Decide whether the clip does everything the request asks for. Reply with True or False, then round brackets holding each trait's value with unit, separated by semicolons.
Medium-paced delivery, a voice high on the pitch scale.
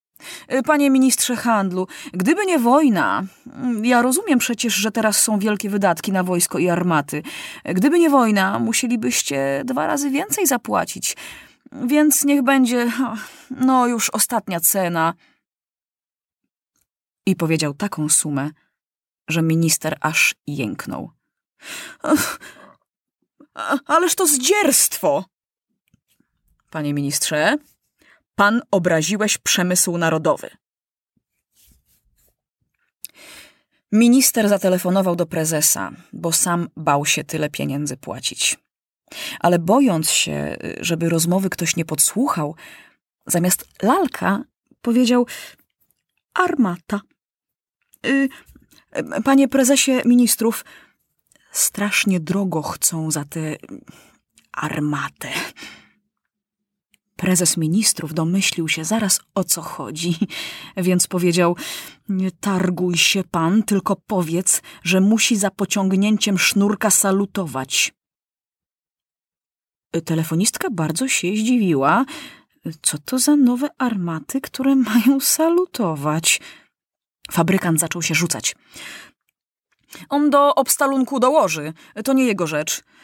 False (95 wpm; 195 Hz)